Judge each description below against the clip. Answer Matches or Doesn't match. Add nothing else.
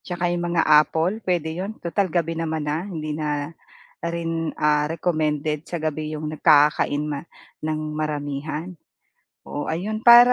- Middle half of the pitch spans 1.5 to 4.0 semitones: Matches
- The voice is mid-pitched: Matches